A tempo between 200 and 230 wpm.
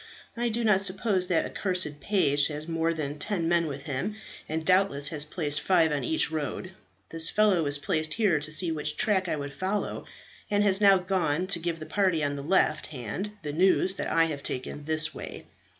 Yes: fast, 205 wpm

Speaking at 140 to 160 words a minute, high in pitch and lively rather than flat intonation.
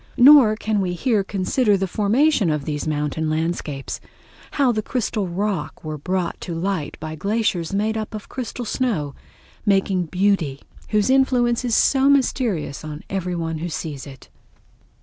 Yes: average, 150 wpm; high, 195 Hz; wide, 5.9 semitones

